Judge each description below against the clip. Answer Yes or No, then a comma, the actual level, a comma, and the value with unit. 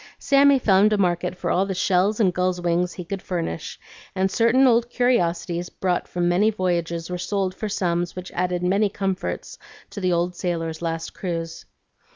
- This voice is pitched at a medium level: Yes, medium, 180 Hz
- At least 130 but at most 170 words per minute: No, average, 180 wpm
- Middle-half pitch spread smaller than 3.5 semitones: Yes, narrow, 2.5 semitones